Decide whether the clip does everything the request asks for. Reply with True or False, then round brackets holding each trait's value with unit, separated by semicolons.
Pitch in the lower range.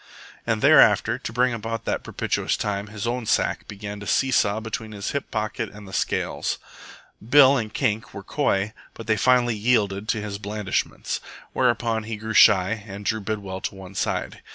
True (110 Hz)